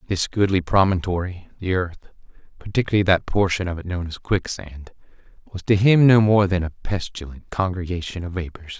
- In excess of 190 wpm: No, average, 150 wpm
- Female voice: No, male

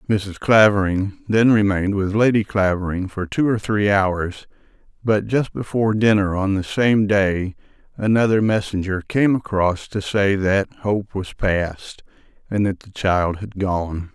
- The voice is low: Yes, low, 100 Hz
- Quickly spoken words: No, average, 155 wpm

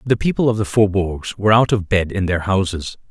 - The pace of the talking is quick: Yes, fast, 230 wpm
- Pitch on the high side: No, low, 100 Hz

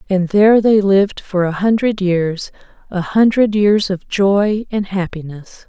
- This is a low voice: No, high, 195 Hz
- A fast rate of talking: No, average, 160 wpm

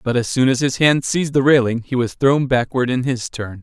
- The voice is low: Yes, low, 130 Hz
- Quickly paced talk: Yes, fast, 265 wpm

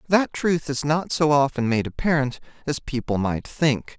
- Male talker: Yes, male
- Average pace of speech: Yes, average, 180 wpm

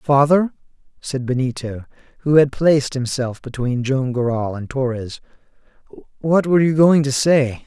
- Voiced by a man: Yes, male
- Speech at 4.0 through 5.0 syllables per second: Yes, 4.7 syllables/s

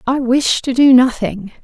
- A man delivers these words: No, female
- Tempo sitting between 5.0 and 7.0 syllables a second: No, 4.3 syllables/s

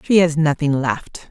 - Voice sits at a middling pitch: Yes, medium, 155 Hz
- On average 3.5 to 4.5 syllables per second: Yes, 4.1 syllables/s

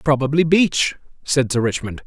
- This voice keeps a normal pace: Yes, average, 145 wpm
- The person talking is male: Yes, male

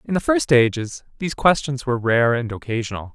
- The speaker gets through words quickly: No, average, 190 wpm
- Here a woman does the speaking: No, male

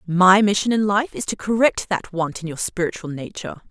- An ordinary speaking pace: No, fast, 210 wpm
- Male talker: No, female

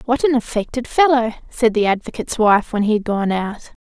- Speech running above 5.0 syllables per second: Yes, 5.5 syllables/s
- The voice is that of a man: No, female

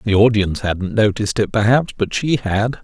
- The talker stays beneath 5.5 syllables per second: Yes, 5.3 syllables/s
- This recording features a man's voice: Yes, male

